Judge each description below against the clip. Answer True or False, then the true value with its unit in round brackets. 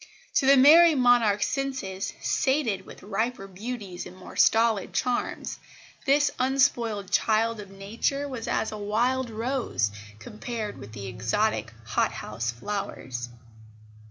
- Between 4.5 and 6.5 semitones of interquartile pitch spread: True (4.8 semitones)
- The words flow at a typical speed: False (125 wpm)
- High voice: True (220 Hz)